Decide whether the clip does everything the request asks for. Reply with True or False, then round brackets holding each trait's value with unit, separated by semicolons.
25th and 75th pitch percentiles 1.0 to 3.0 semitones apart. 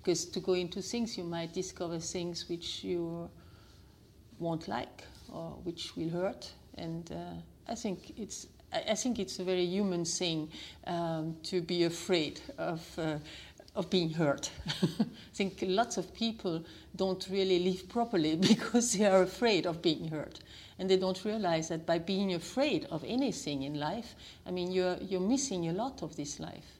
True (2.5 semitones)